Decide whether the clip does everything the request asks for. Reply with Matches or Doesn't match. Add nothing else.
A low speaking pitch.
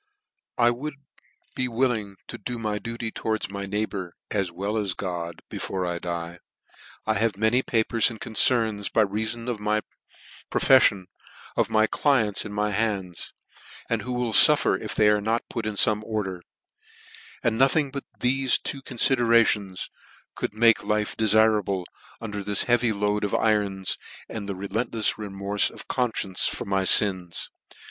Matches